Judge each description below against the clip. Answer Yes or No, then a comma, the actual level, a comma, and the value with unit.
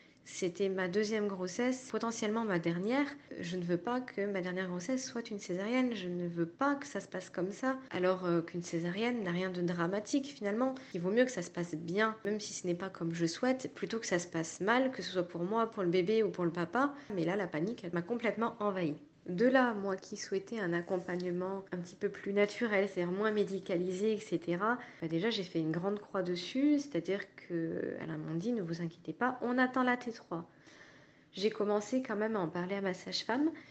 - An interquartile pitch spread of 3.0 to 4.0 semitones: No, average, 4.7 semitones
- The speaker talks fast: Yes, fast, 230 wpm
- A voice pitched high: Yes, high, 195 Hz